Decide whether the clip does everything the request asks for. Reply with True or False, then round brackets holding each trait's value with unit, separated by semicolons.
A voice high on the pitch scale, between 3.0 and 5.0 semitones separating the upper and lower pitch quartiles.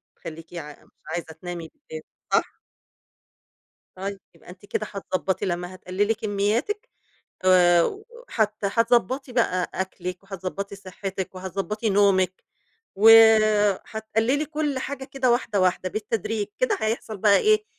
True (200 Hz; 3.5 semitones)